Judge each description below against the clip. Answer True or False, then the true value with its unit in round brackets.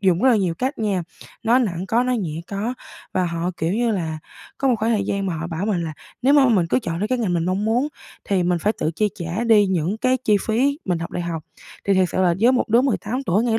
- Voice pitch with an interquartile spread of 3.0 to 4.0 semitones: False (5.3 semitones)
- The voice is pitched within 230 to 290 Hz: False (200 Hz)